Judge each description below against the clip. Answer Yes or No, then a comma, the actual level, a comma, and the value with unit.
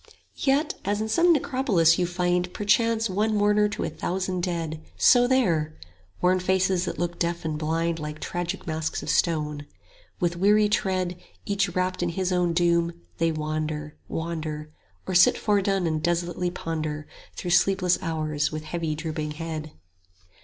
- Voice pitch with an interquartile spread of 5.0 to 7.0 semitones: No, average, 3.2 semitones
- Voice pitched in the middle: Yes, medium, 175 Hz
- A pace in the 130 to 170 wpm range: Yes, average, 160 wpm